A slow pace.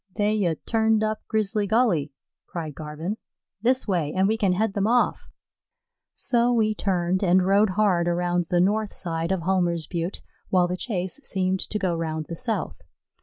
No: average, 170 wpm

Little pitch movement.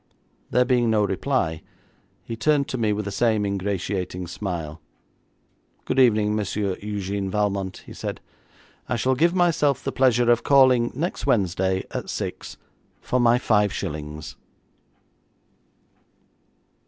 No: average, 4.6 semitones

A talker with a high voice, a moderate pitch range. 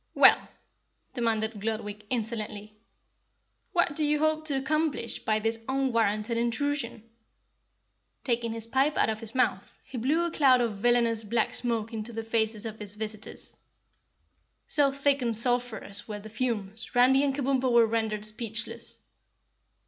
Yes: high, 230 Hz; average, 3.3 semitones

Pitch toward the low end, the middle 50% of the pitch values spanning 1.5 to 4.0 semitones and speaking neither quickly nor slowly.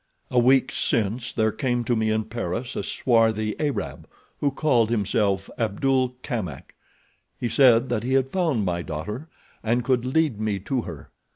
Yes: low, 120 Hz; average, 3.3 semitones; average, 165 wpm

